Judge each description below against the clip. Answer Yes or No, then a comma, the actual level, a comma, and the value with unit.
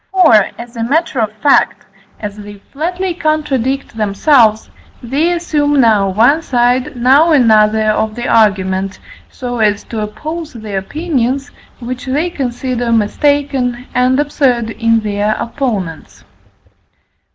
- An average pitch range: Yes, average, 4.9 semitones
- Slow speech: Yes, slow, 125 wpm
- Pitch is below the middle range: No, high, 245 Hz